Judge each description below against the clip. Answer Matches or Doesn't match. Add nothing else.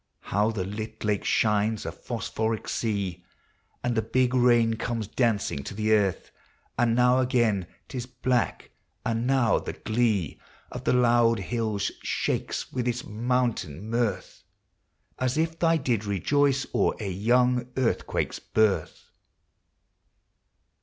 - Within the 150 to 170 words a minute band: Doesn't match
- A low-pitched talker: Matches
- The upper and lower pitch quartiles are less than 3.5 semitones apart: Matches